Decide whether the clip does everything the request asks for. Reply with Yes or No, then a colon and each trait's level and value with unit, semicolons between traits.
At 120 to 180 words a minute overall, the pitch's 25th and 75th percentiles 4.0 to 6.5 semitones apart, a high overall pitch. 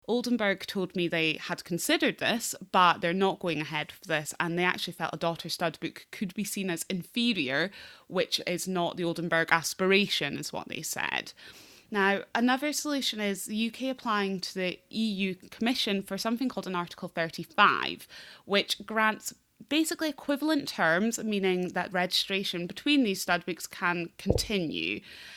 Yes: average, 160 wpm; average, 4.3 semitones; high, 195 Hz